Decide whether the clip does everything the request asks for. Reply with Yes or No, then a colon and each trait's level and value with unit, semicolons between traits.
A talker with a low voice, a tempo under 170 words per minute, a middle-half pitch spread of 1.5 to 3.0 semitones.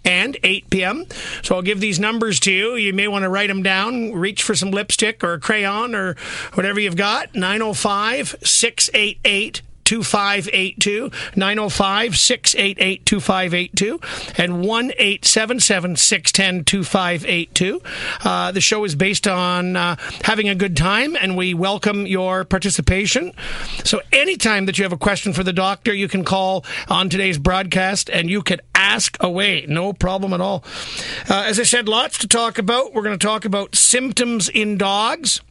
No: high, 195 Hz; average, 160 wpm; narrow, 2.4 semitones